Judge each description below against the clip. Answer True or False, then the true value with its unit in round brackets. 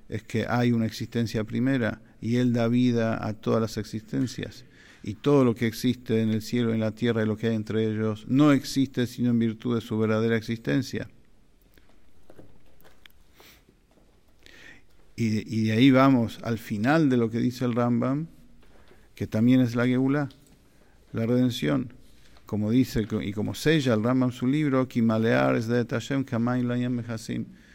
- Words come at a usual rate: True (165 wpm)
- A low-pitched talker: True (115 Hz)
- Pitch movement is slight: True (2.2 semitones)